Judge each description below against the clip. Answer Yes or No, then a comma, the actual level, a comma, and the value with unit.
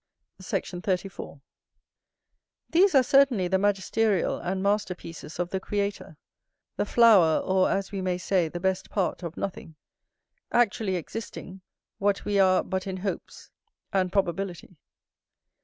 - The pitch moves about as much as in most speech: No, narrow, 2.1 semitones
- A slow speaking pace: Yes, slow, 130 wpm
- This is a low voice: No, high, 190 Hz